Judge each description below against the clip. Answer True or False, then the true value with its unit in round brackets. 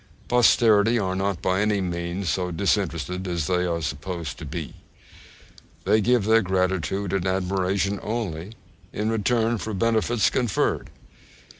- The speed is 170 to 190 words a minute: False (135 wpm)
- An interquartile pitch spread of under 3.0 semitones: False (3.3 semitones)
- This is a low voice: True (95 Hz)